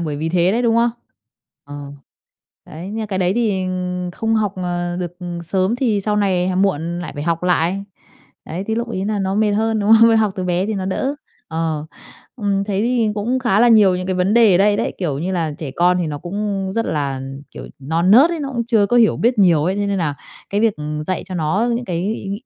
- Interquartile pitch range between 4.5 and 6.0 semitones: No, average, 3.9 semitones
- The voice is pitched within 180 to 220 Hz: Yes, high, 190 Hz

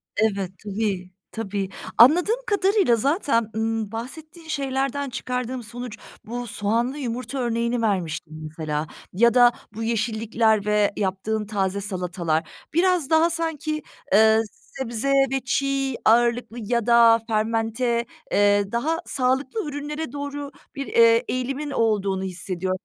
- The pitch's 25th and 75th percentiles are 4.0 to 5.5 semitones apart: Yes, average, 4.6 semitones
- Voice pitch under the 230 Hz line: No, high, 235 Hz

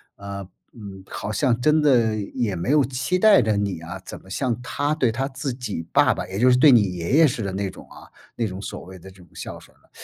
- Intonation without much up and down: No, average, 5.3 semitones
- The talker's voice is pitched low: Yes, low, 115 Hz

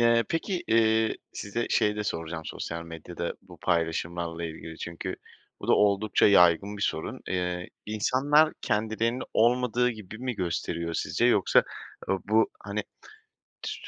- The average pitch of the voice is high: No, low, 100 Hz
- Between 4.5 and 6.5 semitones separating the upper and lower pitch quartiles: Yes, average, 5.1 semitones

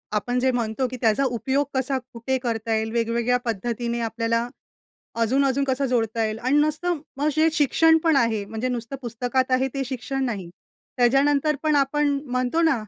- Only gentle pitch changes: No, average, 3.1 semitones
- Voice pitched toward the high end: Yes, very high, 250 Hz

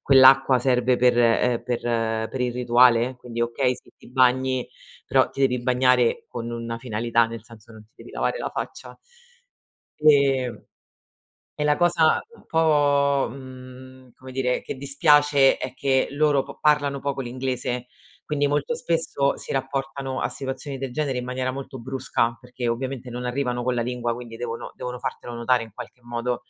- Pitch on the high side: No, low, 130 Hz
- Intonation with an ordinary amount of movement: No, narrow, 2.1 semitones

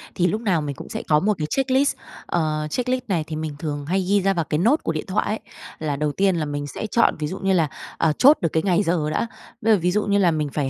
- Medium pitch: Yes, medium, 170 Hz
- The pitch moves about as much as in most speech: Yes, average, 4.9 semitones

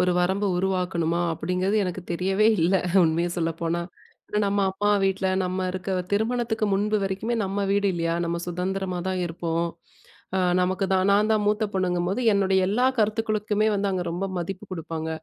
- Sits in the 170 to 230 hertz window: Yes, high, 190 Hz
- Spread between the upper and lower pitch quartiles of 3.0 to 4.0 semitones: No, narrow, 2.5 semitones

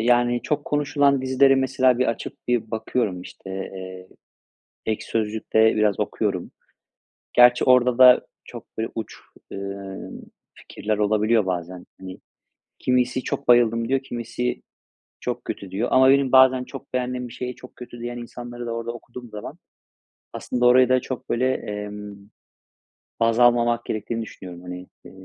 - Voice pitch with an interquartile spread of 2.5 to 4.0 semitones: Yes, average, 3.1 semitones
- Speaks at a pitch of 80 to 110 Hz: No, low, 120 Hz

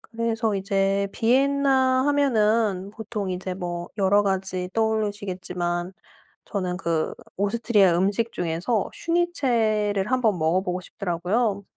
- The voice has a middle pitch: No, high, 205 Hz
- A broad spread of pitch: No, average, 3.9 semitones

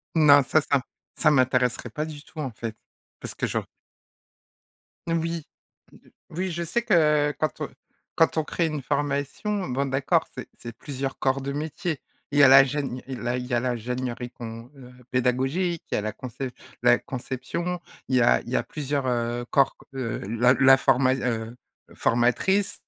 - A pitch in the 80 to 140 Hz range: Yes, low, 135 Hz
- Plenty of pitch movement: No, average, 3.4 semitones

